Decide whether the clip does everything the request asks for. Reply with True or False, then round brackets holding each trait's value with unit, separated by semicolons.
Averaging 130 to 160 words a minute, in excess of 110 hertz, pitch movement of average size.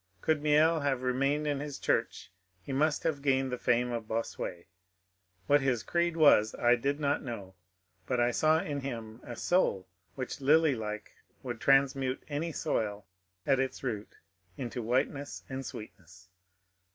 True (155 wpm; 135 Hz; 3.8 semitones)